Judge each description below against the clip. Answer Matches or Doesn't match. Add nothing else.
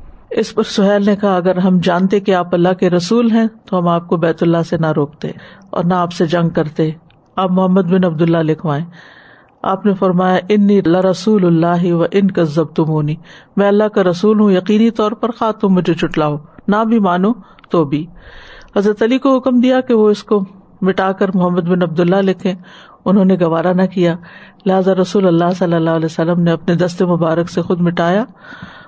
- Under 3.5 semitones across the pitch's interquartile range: Matches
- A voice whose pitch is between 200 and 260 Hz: Doesn't match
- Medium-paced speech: Doesn't match